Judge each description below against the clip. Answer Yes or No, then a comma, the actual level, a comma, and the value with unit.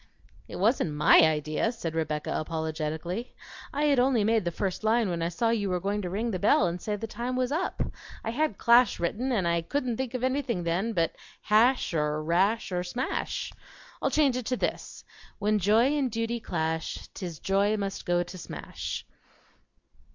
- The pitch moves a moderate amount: No, wide, 5.7 semitones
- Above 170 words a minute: Yes, average, 190 wpm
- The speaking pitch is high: Yes, high, 205 Hz